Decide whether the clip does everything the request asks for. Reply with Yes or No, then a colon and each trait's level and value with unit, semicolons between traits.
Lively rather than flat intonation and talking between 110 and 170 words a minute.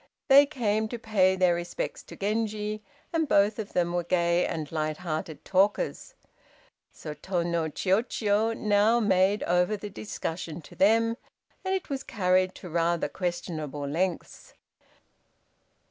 No: average, 3.9 semitones; average, 140 wpm